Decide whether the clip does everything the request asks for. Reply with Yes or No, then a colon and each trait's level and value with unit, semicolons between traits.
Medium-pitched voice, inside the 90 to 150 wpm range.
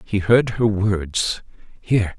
No: low, 100 Hz; slow, 135 wpm